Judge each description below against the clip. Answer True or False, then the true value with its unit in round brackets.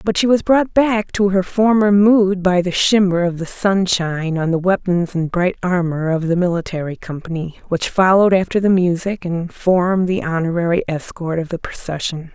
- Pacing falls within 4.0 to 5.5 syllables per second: True (5.0 syllables/s)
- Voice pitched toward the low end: False (185 Hz)